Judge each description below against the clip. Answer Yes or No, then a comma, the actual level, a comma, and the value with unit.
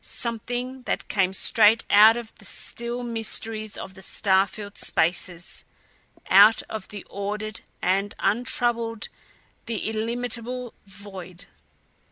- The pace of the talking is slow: Yes, slow, 115 wpm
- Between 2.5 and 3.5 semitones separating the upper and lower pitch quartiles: Yes, average, 2.9 semitones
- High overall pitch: Yes, high, 215 Hz